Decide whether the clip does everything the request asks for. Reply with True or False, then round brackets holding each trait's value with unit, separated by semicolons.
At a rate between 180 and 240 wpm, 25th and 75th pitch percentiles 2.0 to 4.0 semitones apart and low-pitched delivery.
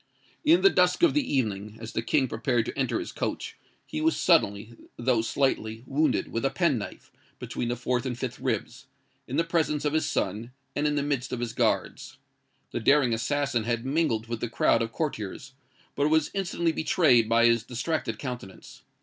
False (190 wpm; 4.8 semitones; 130 Hz)